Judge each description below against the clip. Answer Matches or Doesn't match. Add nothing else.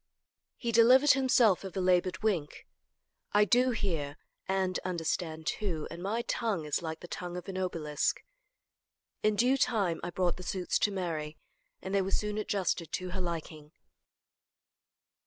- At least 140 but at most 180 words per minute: Matches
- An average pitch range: Matches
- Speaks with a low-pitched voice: Doesn't match